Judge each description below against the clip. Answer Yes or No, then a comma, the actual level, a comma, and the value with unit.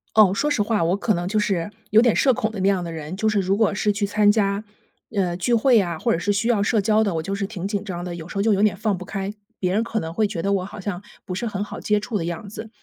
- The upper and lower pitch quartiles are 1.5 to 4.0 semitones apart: Yes, average, 2.8 semitones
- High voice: Yes, high, 200 Hz